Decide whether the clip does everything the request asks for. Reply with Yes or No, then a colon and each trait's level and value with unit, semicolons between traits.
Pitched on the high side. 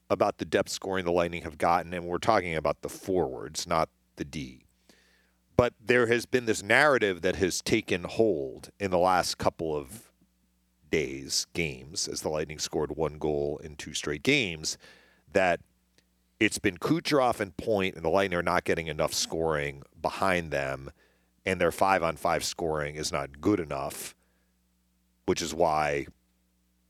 No: very low, 75 Hz